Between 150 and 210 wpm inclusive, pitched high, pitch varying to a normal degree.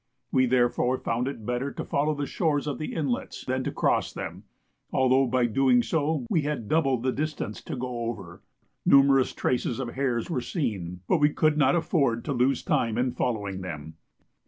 No: average, 185 wpm; low, 130 Hz; average, 3.3 semitones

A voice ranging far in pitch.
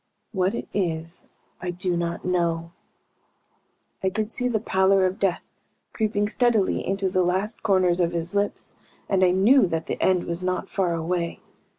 No: narrow, 2.6 semitones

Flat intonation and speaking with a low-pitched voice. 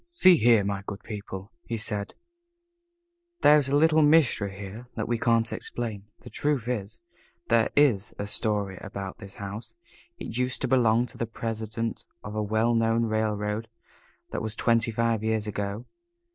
Yes: narrow, 2.3 semitones; low, 110 Hz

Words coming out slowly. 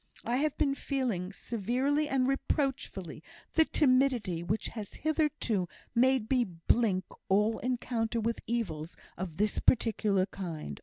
Yes: slow, 125 wpm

